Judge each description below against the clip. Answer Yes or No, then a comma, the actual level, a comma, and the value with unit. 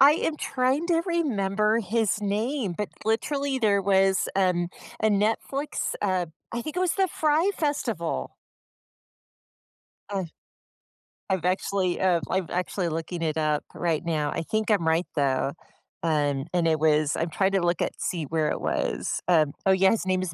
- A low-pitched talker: No, high, 190 Hz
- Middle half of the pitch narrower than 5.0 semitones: No, average, 5.3 semitones